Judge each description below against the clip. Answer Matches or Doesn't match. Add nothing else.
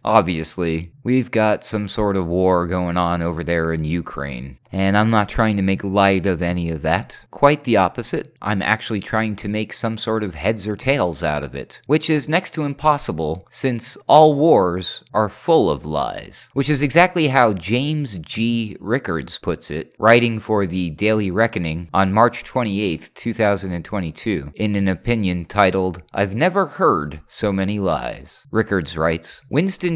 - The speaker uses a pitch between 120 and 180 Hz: Doesn't match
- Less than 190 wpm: Matches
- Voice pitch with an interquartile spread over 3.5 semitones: Matches